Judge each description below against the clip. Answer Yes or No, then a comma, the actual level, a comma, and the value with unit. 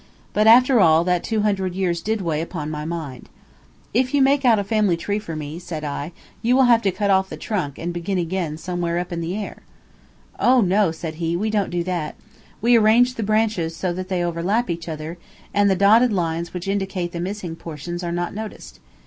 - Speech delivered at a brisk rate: Yes, fast, 215 wpm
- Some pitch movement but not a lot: Yes, average, 4.0 semitones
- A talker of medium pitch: Yes, medium, 180 Hz